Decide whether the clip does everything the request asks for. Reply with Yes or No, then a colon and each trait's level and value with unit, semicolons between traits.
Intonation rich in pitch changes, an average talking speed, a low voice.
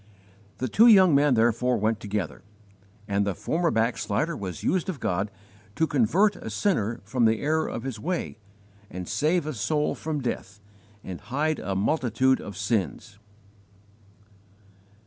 Yes: wide, 7.2 semitones; average, 145 wpm; low, 125 Hz